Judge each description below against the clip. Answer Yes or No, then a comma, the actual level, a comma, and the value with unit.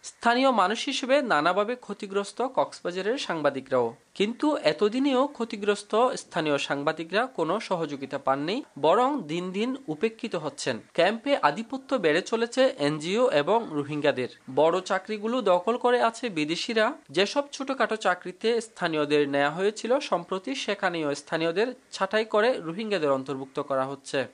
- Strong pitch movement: Yes, wide, 7.4 semitones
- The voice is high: Yes, high, 205 Hz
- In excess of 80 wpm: Yes, fast, 120 wpm